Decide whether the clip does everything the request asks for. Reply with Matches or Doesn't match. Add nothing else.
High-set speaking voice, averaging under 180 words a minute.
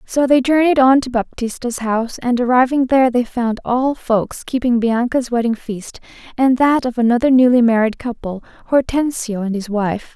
Matches